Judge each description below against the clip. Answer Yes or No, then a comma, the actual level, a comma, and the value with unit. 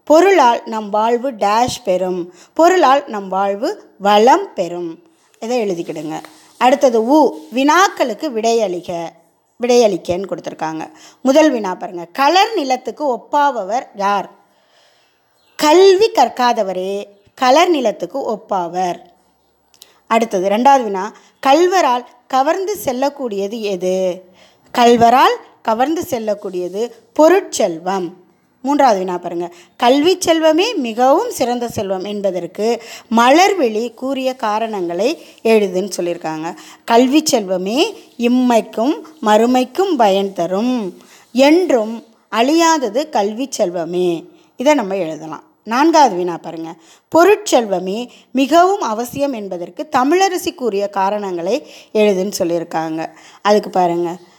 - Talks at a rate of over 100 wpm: No, average, 90 wpm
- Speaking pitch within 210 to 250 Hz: Yes, high, 230 Hz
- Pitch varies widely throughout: Yes, wide, 7.1 semitones